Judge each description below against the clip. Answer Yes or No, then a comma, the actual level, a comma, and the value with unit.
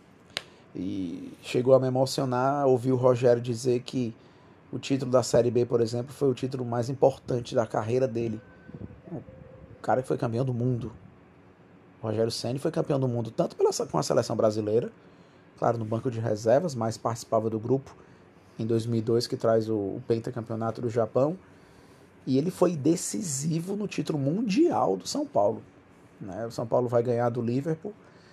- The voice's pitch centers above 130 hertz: No, low, 120 Hz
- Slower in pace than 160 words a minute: No, average, 170 wpm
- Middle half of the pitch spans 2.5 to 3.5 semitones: Yes, average, 3.0 semitones